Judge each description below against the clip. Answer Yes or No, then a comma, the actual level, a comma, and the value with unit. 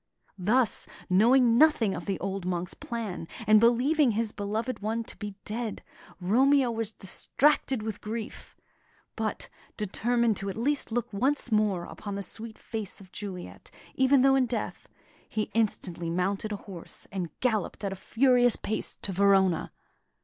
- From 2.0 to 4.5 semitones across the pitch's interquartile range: Yes, average, 3.6 semitones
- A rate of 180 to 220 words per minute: No, average, 155 wpm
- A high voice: Yes, high, 215 Hz